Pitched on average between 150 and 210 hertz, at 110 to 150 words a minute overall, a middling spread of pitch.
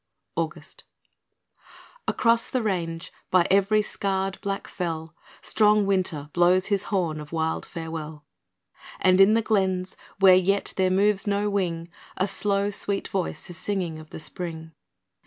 Yes: high, 190 Hz; average, 140 wpm; average, 3.3 semitones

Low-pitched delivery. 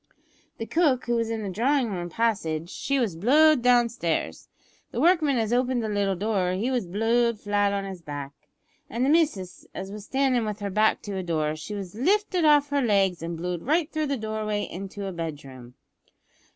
No: high, 215 Hz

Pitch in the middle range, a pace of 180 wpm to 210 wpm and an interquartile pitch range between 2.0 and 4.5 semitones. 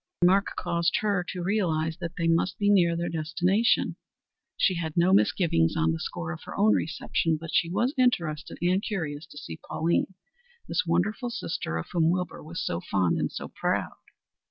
Yes: medium, 170 Hz; average, 185 wpm; average, 3.4 semitones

